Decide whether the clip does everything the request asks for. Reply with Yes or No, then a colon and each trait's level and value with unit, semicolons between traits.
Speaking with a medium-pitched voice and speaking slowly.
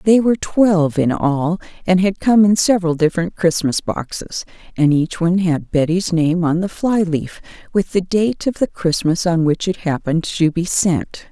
No: medium, 175 Hz; average, 190 wpm